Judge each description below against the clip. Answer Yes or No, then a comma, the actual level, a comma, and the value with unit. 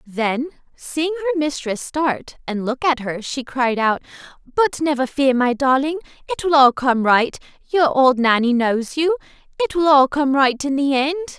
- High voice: Yes, very high, 280 Hz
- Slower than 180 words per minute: No, average, 185 wpm